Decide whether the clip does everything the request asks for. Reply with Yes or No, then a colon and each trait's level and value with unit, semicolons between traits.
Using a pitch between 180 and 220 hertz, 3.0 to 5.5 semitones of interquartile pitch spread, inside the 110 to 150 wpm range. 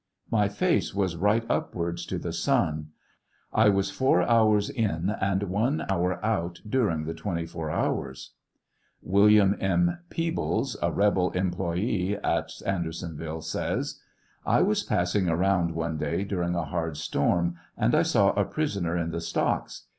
No: very low, 90 Hz; average, 3.5 semitones; average, 145 wpm